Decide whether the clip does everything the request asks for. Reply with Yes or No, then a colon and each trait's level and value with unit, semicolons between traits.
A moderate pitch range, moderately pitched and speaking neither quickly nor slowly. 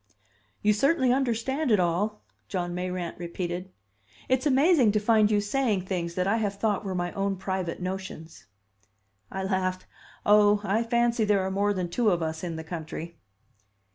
No: average, 3.5 semitones; high, 195 Hz; average, 170 wpm